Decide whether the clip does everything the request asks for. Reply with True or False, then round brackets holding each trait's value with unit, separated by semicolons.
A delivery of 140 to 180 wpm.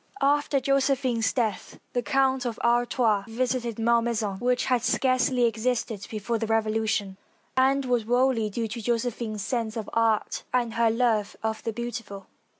True (150 wpm)